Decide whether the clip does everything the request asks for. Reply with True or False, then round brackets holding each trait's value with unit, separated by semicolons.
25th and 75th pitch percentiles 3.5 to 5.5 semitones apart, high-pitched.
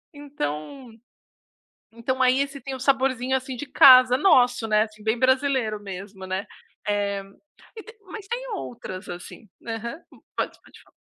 True (4.2 semitones; 250 Hz)